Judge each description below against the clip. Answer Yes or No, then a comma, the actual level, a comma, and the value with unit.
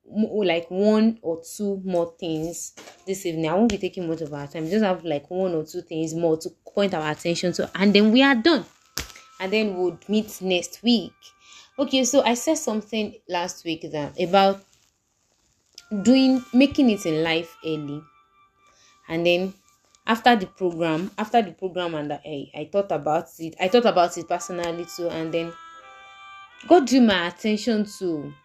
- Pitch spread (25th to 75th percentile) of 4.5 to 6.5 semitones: Yes, average, 4.9 semitones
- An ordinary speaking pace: Yes, average, 175 wpm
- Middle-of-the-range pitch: Yes, medium, 180 Hz